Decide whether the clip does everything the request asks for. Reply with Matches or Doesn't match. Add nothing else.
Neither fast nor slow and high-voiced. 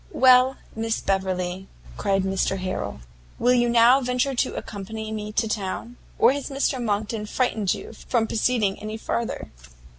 Matches